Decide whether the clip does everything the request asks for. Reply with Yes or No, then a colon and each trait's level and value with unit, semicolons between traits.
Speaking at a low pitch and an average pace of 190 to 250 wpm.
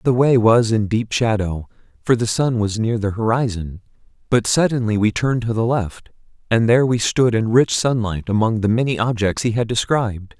Yes: low, 115 Hz; average, 195 wpm